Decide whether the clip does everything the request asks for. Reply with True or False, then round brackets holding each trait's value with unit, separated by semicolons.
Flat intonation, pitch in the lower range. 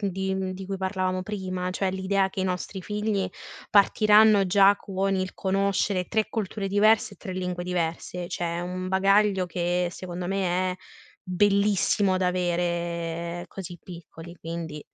False (1.8 semitones; 185 Hz)